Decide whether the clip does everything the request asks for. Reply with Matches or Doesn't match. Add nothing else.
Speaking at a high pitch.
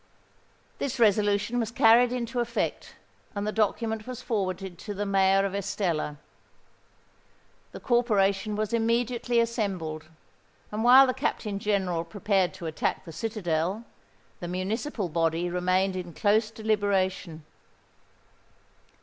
Matches